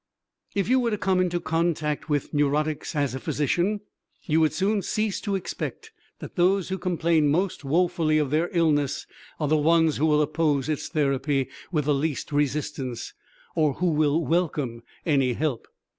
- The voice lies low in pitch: No, medium, 155 Hz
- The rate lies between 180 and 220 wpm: No, average, 170 wpm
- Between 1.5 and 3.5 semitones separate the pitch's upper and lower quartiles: Yes, average, 3.1 semitones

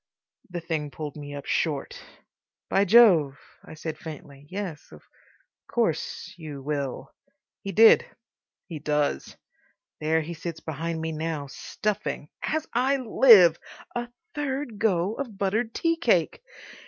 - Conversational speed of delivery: No, slow, 120 wpm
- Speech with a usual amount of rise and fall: No, wide, 6.4 semitones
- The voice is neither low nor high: Yes, medium, 170 Hz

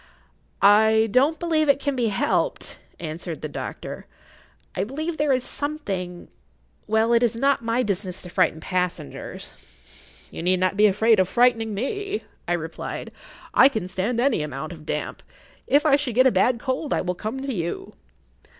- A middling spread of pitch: No, wide, 6.9 semitones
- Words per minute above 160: Yes, average, 170 wpm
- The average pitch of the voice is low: No, high, 220 Hz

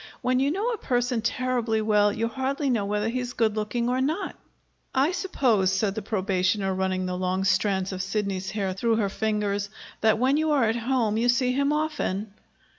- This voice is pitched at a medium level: No, high, 220 Hz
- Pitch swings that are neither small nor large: Yes, average, 4.3 semitones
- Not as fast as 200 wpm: Yes, average, 190 wpm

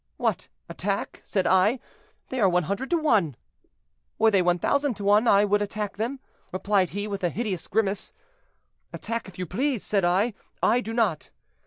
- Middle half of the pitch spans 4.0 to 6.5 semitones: No, average, 3.4 semitones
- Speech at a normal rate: Yes, average, 170 wpm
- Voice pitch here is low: No, high, 205 Hz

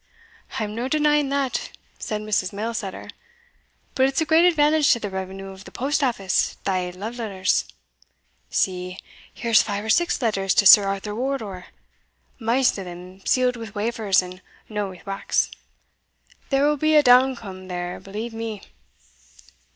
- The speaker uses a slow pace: No, average, 150 wpm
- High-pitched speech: Yes, high, 215 Hz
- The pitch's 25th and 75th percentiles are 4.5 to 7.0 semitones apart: Yes, average, 5.2 semitones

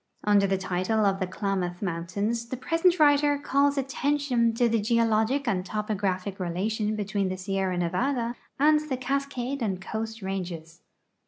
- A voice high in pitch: Yes, high, 215 Hz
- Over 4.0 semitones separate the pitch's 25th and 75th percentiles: Yes, wide, 5.4 semitones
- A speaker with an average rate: Yes, average, 150 wpm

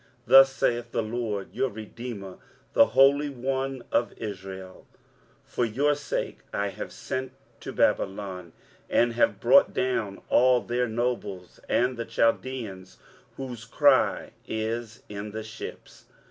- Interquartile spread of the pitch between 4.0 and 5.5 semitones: No, average, 3.6 semitones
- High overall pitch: No, low, 115 Hz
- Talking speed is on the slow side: Yes, slow, 130 wpm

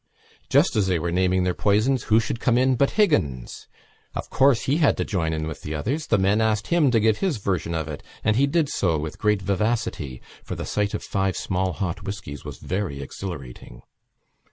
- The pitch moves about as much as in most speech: No, wide, 5.8 semitones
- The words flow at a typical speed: No, fast, 210 wpm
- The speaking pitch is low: Yes, low, 100 Hz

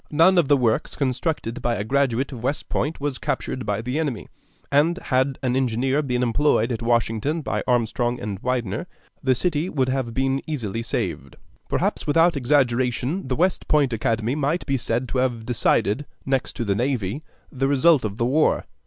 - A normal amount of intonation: Yes, average, 3.6 semitones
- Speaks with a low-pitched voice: Yes, low, 130 Hz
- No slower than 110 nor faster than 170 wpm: No, average, 180 wpm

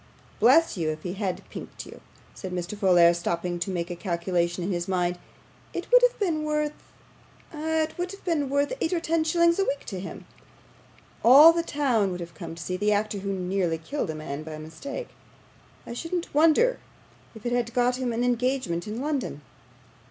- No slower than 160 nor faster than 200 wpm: Yes, average, 195 wpm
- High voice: Yes, high, 220 Hz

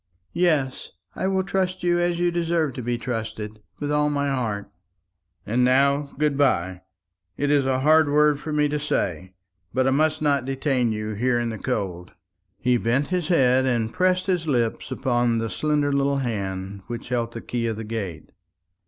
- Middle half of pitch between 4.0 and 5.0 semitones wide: Yes, average, 4.6 semitones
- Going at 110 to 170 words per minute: No, average, 185 wpm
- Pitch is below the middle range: Yes, low, 130 Hz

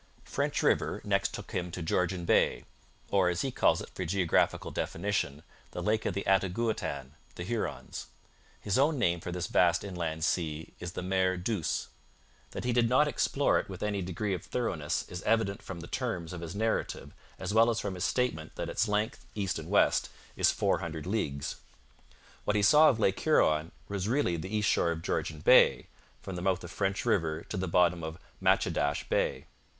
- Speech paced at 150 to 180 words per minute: No, average, 190 wpm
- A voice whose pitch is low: Yes, very low, 95 Hz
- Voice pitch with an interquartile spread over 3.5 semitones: Yes, average, 3.9 semitones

